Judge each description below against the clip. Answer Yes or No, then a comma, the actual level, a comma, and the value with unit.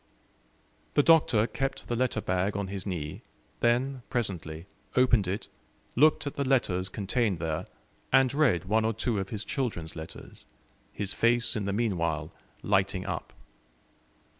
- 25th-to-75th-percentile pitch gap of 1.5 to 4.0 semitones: No, average, 5.2 semitones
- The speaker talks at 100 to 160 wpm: Yes, average, 145 wpm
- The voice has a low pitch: Yes, low, 105 Hz